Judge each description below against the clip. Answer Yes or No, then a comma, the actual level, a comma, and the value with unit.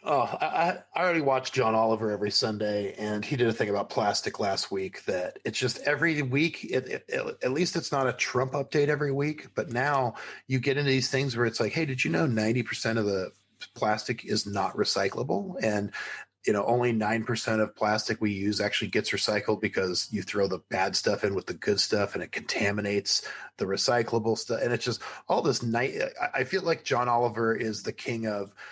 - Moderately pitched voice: No, low, 115 Hz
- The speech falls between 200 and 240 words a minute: Yes, fast, 205 wpm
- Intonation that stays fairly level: No, average, 4.2 semitones